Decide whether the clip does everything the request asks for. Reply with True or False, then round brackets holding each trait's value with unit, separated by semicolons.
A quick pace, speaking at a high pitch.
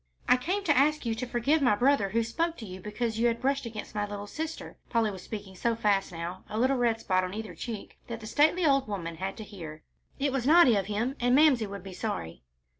True (240 wpm; 225 Hz)